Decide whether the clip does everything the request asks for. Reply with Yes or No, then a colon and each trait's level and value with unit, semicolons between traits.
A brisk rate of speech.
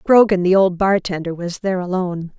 No: average, 175 wpm